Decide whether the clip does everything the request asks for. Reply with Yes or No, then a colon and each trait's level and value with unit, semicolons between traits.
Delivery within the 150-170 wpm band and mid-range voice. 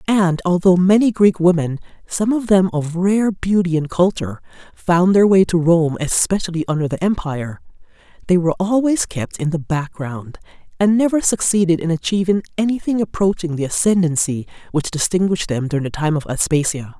Yes: average, 160 wpm; medium, 175 Hz